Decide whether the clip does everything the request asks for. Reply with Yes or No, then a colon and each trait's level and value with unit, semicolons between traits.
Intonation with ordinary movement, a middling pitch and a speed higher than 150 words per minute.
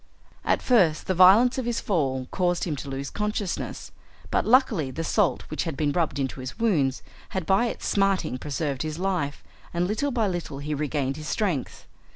No: wide, 6.0 semitones; medium, 170 Hz; average, 190 wpm